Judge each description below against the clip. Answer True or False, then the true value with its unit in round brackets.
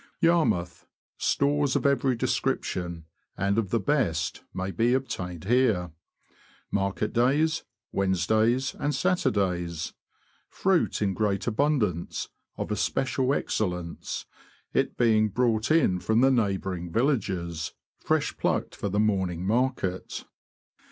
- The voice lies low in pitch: True (110 Hz)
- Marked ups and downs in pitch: True (6.2 semitones)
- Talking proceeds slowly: True (120 wpm)